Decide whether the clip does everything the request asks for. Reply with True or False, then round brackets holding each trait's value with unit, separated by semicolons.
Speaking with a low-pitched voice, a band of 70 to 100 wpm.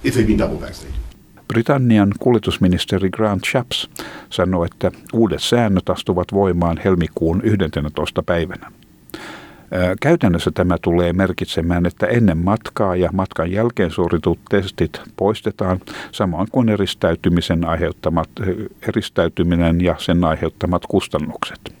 True (90 Hz; 95 wpm)